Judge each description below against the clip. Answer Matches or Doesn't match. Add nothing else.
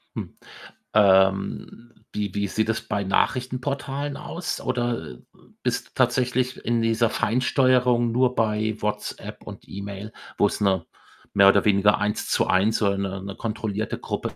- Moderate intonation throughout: Matches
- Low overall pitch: Matches